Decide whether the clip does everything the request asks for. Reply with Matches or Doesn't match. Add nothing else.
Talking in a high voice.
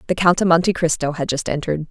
Doesn't match